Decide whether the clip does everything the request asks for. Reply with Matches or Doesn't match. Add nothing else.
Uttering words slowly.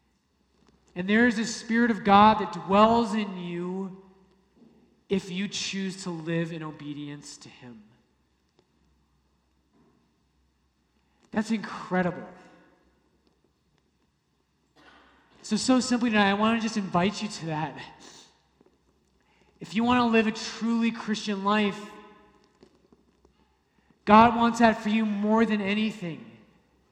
Matches